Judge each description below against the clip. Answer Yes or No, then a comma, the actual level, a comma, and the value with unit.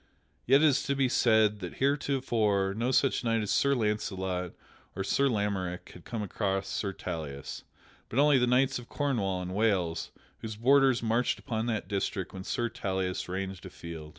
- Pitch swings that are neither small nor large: Yes, average, 4.8 semitones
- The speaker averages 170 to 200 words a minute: Yes, average, 175 wpm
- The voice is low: Yes, low, 105 Hz